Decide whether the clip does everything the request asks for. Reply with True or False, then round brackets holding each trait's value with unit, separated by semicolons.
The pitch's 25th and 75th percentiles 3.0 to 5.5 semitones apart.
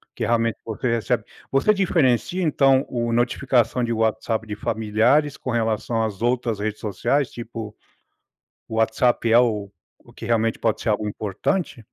False (2.4 semitones)